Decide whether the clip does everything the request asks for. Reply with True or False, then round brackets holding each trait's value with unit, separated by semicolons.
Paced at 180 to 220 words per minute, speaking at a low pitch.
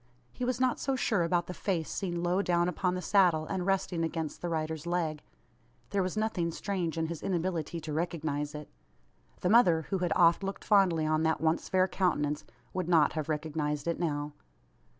False (190 wpm; 170 Hz)